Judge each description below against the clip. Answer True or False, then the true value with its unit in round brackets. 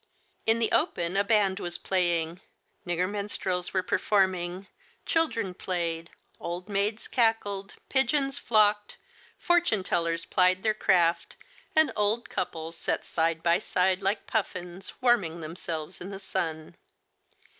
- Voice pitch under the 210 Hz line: True (190 Hz)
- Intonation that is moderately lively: True (3.5 semitones)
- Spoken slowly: True (130 wpm)